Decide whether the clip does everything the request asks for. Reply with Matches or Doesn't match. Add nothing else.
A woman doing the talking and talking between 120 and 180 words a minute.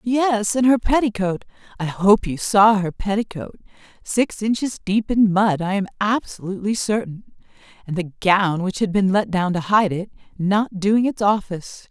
Matches